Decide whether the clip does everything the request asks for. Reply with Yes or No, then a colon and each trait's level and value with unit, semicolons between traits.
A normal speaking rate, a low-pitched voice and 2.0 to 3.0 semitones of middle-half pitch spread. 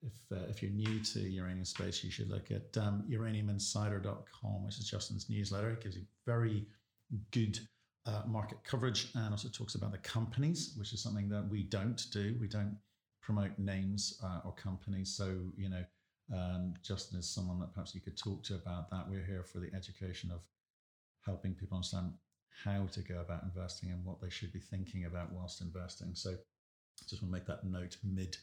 Yes: average, 195 wpm; low, 100 Hz; narrow, 2.6 semitones